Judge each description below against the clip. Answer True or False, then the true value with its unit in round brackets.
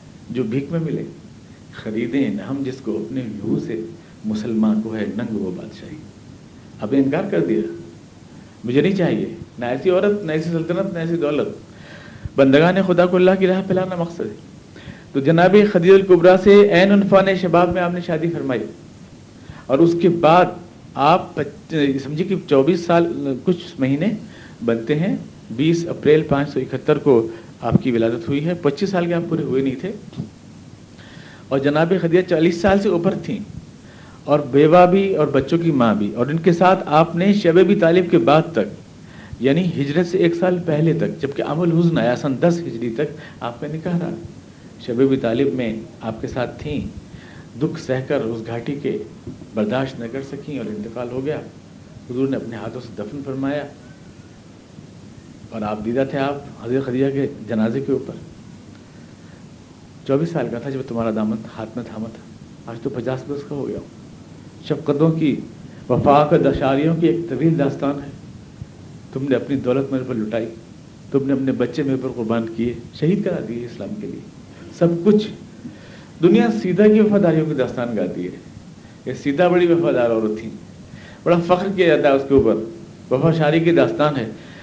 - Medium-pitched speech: True (145 Hz)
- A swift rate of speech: False (180 wpm)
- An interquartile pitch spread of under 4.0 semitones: False (5.6 semitones)